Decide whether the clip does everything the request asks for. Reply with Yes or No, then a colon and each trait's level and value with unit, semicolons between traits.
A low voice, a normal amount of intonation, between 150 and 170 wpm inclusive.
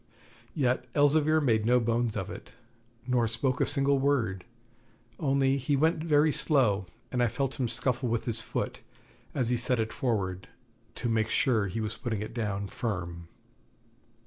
Yes: low, 120 Hz; average, 3.9 semitones; average, 165 wpm